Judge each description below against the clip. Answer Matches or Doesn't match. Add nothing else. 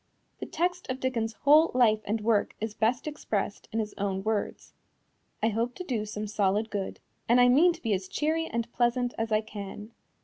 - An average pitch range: Matches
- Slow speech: Doesn't match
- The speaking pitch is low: Doesn't match